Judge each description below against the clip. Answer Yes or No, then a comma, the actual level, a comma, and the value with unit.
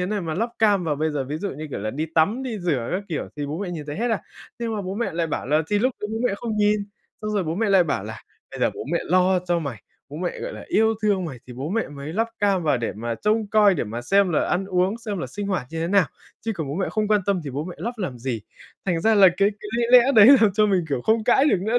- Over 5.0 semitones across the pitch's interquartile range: Yes, wide, 5.5 semitones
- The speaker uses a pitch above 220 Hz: No, medium, 185 Hz